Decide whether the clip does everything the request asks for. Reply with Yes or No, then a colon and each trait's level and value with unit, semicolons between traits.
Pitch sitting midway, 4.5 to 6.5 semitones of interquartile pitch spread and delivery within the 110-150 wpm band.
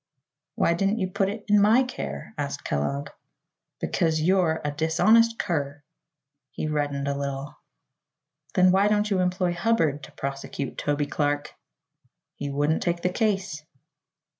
Yes: medium, 160 Hz; average, 5.3 semitones; average, 140 wpm